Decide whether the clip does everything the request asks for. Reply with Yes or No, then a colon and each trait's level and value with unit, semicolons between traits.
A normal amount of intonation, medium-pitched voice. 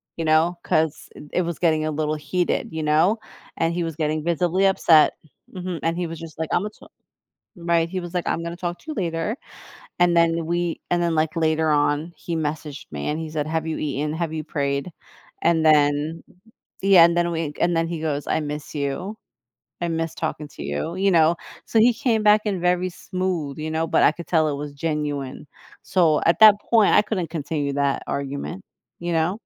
No: narrow, 2.3 semitones; medium, 165 Hz